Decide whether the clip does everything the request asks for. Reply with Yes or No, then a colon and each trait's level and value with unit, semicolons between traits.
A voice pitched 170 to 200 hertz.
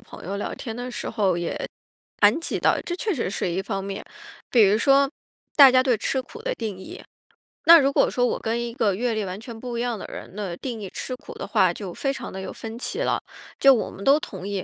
No: high, 230 Hz